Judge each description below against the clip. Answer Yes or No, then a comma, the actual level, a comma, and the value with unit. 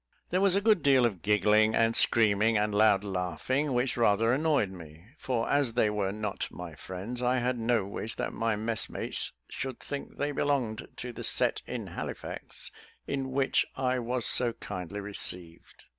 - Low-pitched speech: Yes, low, 115 Hz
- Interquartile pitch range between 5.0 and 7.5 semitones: No, average, 3.9 semitones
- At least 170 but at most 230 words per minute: Yes, average, 175 wpm